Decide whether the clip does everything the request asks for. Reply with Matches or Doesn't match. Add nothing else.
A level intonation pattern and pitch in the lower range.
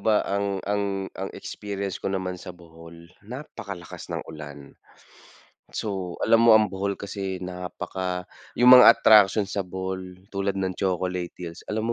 Matches